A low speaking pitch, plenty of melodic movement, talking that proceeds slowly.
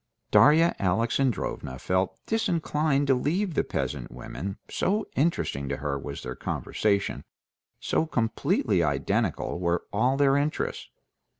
Yes: low, 125 Hz; wide, 8.8 semitones; slow, 120 wpm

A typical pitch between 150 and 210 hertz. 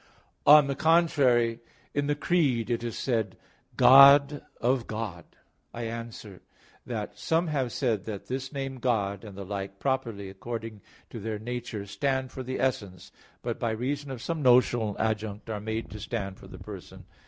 No: low, 115 Hz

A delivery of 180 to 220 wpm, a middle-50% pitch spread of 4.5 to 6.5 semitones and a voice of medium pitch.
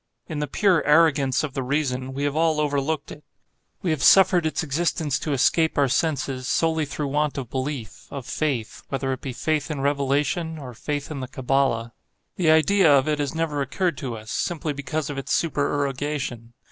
No: average, 185 wpm; average, 2.8 semitones; medium, 145 Hz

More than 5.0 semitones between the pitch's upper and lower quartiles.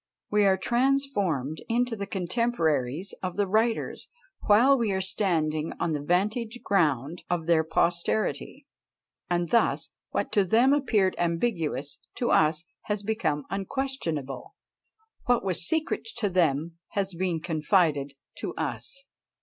Yes: wide, 5.6 semitones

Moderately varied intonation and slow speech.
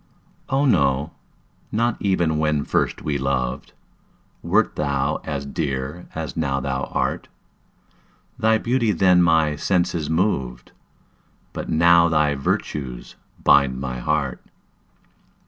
Yes: average, 4.1 semitones; slow, 110 wpm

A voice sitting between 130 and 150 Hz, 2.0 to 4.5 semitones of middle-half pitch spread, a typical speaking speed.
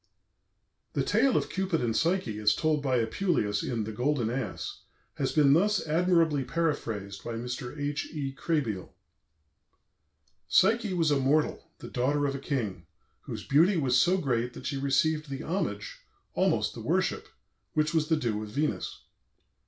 No: medium, 140 Hz; average, 5.1 semitones; average, 160 wpm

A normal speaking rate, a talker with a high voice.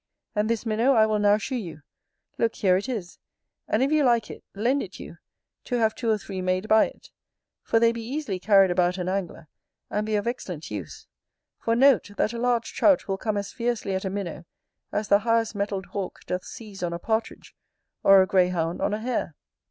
No: fast, 215 wpm; high, 210 Hz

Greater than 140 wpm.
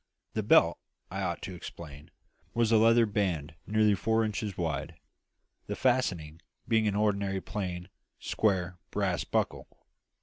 No: slow, 135 wpm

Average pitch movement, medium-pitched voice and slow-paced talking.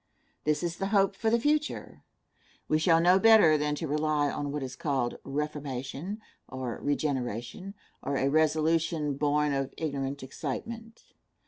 No: average, 3.8 semitones; medium, 150 Hz; average, 145 wpm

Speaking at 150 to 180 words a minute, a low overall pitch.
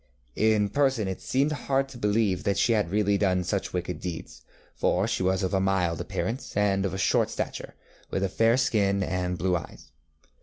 No: average, 190 wpm; low, 100 Hz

